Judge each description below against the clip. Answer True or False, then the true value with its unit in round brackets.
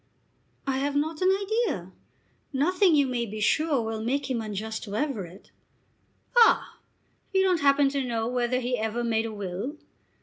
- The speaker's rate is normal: True (165 wpm)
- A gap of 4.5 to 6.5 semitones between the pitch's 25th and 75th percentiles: True (5.2 semitones)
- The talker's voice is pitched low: False (255 Hz)